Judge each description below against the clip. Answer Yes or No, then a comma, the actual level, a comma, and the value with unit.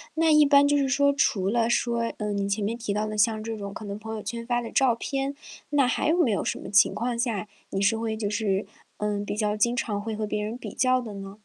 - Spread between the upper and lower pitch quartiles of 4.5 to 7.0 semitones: No, average, 3.1 semitones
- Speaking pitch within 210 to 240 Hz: Yes, high, 220 Hz